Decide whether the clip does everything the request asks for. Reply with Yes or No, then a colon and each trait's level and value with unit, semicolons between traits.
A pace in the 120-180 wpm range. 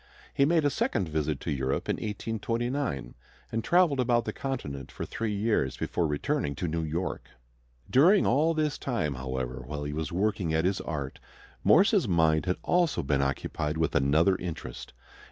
Yes: average, 170 wpm